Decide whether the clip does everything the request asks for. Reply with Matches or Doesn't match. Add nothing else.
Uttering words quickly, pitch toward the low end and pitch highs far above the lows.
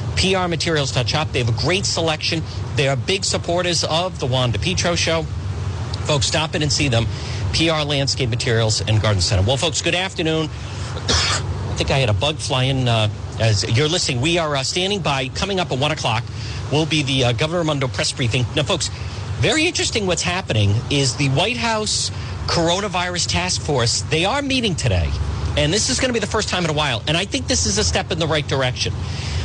Matches